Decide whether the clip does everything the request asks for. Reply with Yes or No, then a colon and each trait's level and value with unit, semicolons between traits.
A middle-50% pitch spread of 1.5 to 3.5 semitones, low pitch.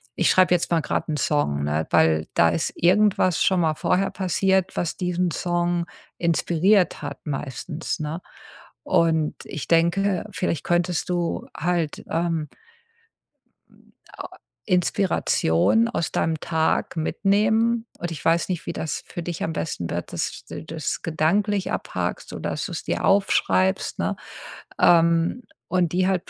No: average, 2.7 semitones; medium, 170 Hz